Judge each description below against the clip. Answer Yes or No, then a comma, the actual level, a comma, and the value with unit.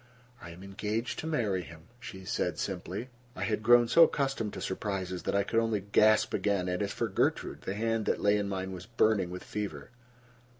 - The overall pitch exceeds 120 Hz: No, low, 105 Hz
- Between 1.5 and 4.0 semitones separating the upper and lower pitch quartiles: Yes, average, 3.1 semitones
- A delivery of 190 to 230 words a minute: Yes, fast, 205 wpm